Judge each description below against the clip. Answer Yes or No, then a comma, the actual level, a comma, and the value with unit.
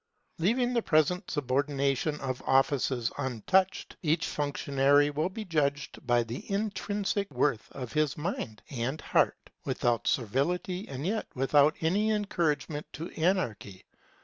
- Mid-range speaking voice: Yes, medium, 145 Hz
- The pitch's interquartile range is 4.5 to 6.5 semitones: Yes, wide, 5.4 semitones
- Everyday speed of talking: No, slow, 125 wpm